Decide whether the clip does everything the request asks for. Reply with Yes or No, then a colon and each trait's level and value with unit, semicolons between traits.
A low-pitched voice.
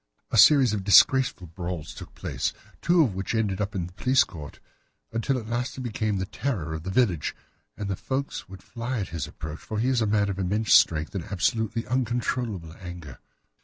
Yes: low, 105 Hz